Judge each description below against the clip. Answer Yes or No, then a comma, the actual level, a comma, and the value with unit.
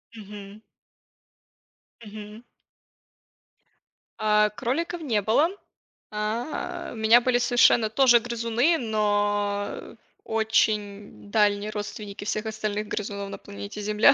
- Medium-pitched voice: No, high, 215 Hz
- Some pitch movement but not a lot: No, narrow, 2.1 semitones